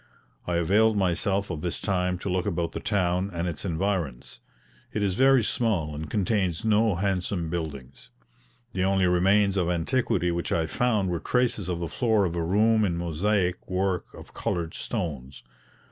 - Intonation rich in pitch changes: No, average, 3.2 semitones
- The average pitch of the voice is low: Yes, very low, 90 Hz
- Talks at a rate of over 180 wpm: No, average, 170 wpm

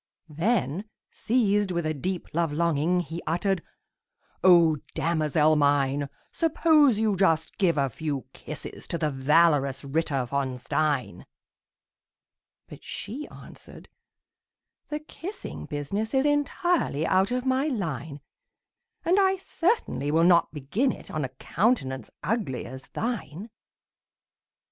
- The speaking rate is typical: No, slow, 120 wpm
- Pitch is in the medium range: Yes, medium, 170 Hz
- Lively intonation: Yes, wide, 7.5 semitones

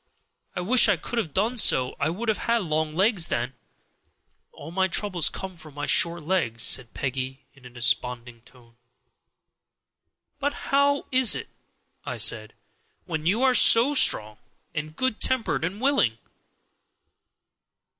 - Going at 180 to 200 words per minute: No, average, 145 wpm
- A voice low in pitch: No, medium, 170 Hz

